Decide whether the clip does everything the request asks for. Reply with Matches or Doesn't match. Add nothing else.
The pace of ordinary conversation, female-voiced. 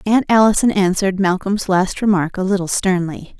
Matches